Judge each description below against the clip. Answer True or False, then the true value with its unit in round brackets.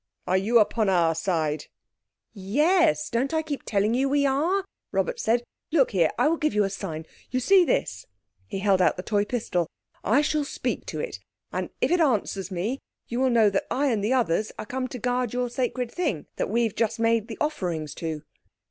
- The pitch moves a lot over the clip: True (6.0 semitones)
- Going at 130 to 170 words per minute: False (200 wpm)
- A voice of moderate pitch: False (230 Hz)